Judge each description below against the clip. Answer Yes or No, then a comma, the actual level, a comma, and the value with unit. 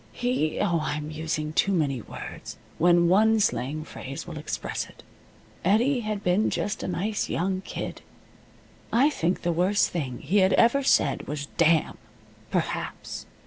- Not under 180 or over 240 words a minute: No, average, 155 wpm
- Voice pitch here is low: No, medium, 175 Hz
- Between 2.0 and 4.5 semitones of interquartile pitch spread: No, average, 5.1 semitones